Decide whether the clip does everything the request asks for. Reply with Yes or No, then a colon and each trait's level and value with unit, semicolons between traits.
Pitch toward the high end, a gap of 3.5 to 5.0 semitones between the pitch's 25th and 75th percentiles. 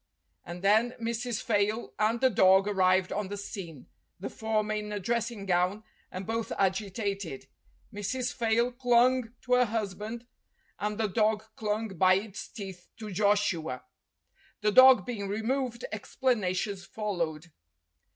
No: high, 210 Hz; average, 3.1 semitones